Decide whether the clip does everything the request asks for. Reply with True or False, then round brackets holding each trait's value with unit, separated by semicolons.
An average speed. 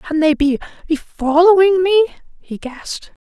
False (130 wpm)